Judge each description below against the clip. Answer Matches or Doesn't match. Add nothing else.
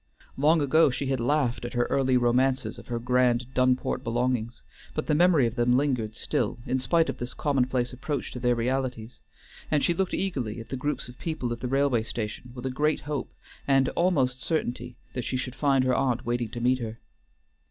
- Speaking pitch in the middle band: Doesn't match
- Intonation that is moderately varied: Doesn't match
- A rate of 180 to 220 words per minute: Matches